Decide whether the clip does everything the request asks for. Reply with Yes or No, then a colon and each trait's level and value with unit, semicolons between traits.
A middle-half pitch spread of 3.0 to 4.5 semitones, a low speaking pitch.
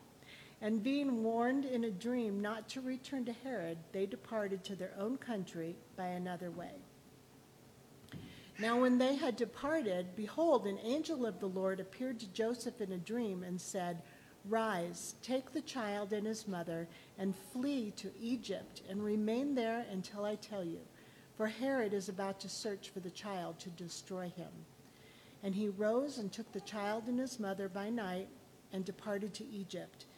No: average, 3.8 semitones; high, 205 Hz